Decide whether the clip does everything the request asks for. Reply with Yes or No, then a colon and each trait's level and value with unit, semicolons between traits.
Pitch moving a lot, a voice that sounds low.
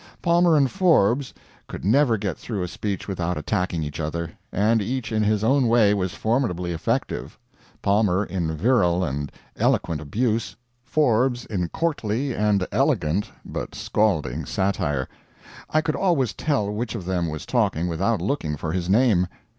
Yes: wide, 5.9 semitones; low, 105 Hz